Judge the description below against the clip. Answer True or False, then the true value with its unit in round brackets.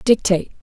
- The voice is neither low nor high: False (200 Hz)